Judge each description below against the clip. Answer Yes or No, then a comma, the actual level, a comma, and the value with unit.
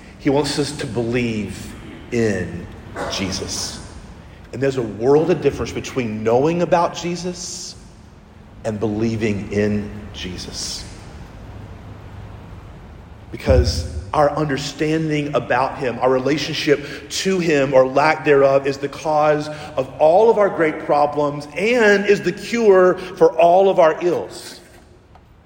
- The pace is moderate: No, slow, 120 wpm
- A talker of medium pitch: No, low, 130 Hz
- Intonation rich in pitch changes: Yes, wide, 6.9 semitones